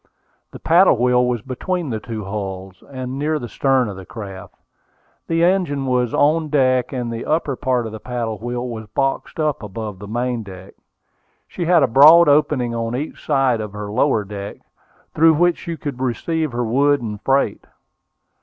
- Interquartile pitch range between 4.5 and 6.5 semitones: Yes, average, 4.8 semitones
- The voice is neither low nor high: No, low, 125 Hz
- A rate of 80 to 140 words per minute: No, average, 180 wpm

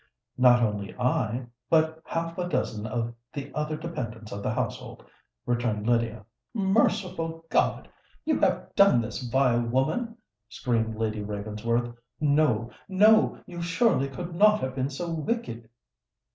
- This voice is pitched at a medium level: No, low, 130 Hz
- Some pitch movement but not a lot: No, wide, 6.2 semitones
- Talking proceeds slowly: Yes, slow, 130 wpm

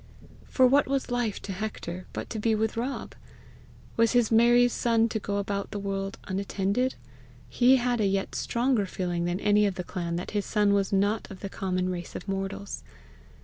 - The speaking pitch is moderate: No, high, 205 Hz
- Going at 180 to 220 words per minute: Yes, average, 190 wpm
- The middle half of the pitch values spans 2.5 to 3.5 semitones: Yes, average, 3.2 semitones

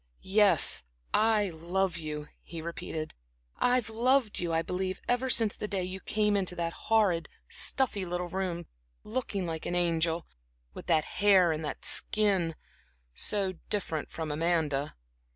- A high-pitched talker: No, medium, 180 Hz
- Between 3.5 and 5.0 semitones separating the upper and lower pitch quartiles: Yes, average, 4.0 semitones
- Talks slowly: No, average, 145 wpm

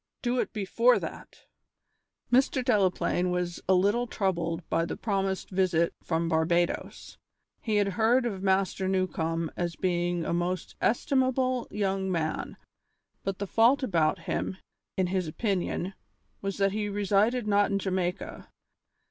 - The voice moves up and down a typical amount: Yes, average, 3.2 semitones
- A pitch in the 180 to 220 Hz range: Yes, high, 190 Hz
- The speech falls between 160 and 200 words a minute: No, average, 140 wpm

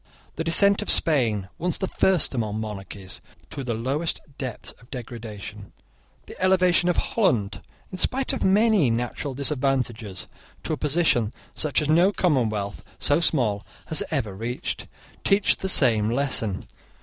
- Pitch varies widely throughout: Yes, wide, 7.5 semitones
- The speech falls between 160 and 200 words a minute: No, average, 145 wpm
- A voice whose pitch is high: No, low, 135 Hz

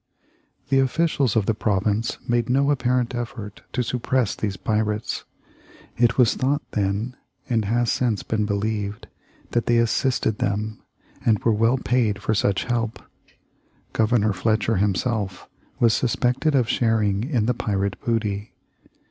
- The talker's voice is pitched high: No, low, 115 Hz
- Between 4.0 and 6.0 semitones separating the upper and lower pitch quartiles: No, average, 2.9 semitones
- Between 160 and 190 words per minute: No, average, 140 wpm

